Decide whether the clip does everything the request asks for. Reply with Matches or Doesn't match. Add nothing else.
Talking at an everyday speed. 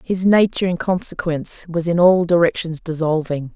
Matches